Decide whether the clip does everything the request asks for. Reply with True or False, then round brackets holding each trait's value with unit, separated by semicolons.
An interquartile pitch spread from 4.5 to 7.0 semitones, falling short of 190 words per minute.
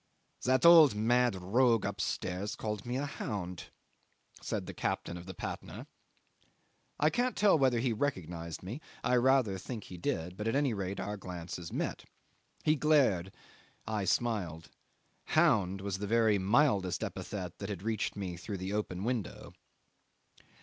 True (5.0 semitones; 150 wpm)